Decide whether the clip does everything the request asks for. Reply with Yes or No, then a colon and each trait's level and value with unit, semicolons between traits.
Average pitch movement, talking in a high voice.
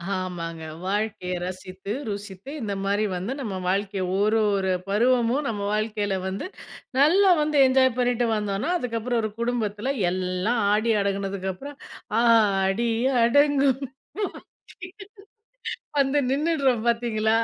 Yes: average, 4.1 semitones; high, 215 Hz